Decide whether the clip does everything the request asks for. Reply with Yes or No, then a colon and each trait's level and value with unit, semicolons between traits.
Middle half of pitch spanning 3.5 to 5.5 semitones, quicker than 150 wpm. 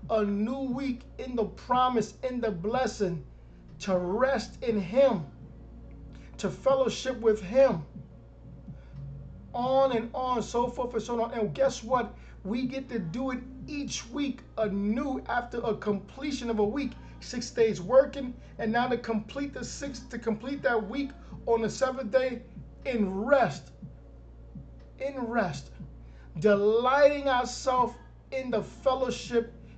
No: average, 3.9 semitones; slow, 135 wpm